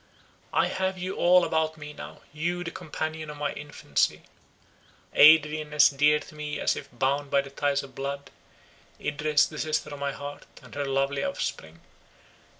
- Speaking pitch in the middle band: Yes, medium, 150 Hz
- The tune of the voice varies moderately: No, narrow, 1.9 semitones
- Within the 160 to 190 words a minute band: Yes, average, 165 wpm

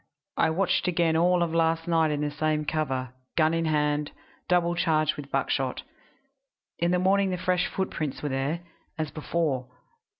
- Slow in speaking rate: No, average, 165 wpm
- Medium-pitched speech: Yes, medium, 160 Hz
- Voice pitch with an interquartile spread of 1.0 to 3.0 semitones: Yes, narrow, 2.6 semitones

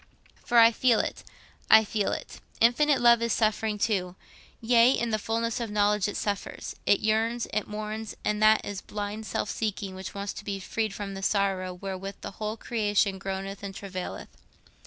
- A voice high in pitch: Yes, high, 210 Hz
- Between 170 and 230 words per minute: Yes, average, 180 wpm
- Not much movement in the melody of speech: Yes, narrow, 2.2 semitones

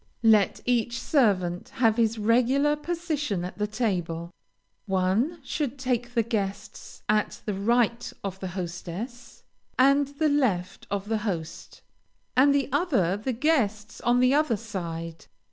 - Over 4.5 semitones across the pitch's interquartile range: Yes, average, 5.2 semitones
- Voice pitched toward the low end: No, high, 225 Hz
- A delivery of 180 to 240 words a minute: No, slow, 135 wpm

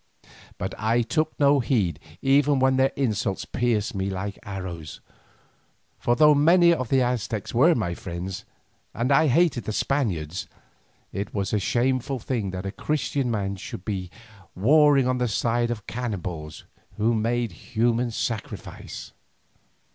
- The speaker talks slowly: No, average, 145 wpm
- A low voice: Yes, low, 115 Hz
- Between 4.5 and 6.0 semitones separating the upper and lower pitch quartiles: Yes, average, 5.1 semitones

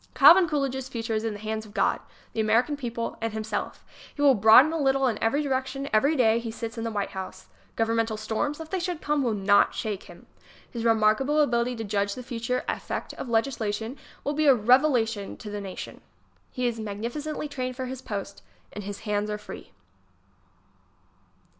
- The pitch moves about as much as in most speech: Yes, average, 3.9 semitones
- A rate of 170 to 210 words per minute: Yes, average, 190 wpm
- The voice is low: No, high, 230 Hz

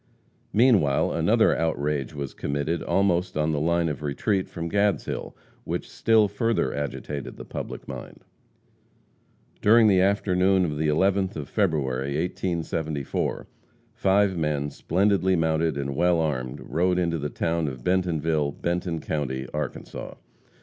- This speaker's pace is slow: Yes, slow, 130 wpm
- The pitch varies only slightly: No, average, 4.3 semitones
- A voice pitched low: Yes, very low, 80 Hz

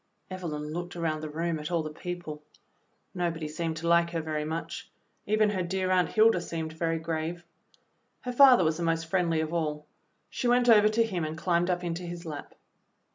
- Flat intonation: Yes, narrow, 2.2 semitones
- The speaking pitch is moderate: Yes, medium, 170 Hz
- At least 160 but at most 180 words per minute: No, average, 195 wpm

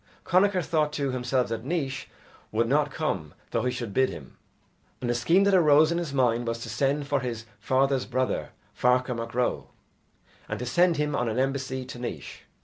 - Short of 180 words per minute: No, average, 195 wpm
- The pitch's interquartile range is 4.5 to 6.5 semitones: No, average, 3.6 semitones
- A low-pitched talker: Yes, low, 130 Hz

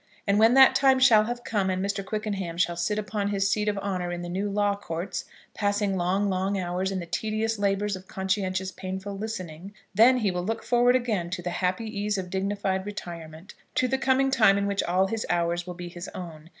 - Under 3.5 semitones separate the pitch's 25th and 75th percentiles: Yes, average, 2.7 semitones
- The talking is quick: Yes, fast, 215 wpm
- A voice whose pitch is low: No, high, 195 Hz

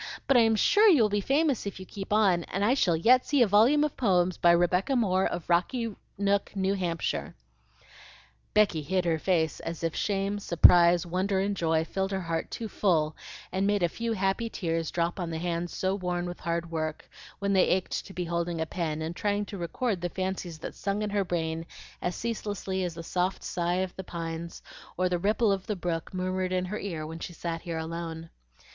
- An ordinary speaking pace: No, fast, 215 wpm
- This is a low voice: No, medium, 185 Hz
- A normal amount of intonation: Yes, average, 3.1 semitones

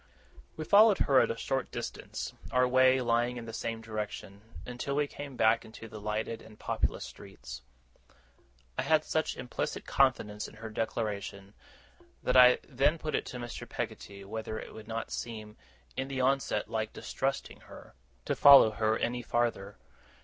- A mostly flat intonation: No, average, 3.3 semitones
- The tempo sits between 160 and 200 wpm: Yes, average, 165 wpm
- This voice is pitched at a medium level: No, low, 115 Hz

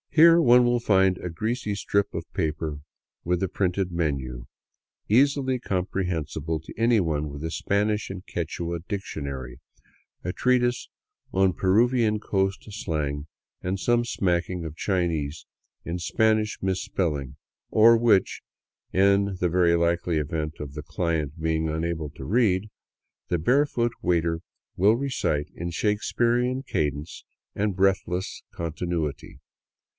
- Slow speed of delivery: Yes, slow, 130 wpm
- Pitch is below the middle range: Yes, very low, 90 Hz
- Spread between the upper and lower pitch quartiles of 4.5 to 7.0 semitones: Yes, average, 5.0 semitones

